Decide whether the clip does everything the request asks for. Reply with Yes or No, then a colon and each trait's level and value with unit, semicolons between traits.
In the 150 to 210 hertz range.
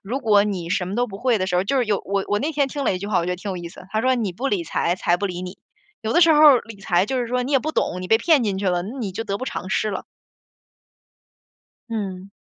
Yes: high, 205 Hz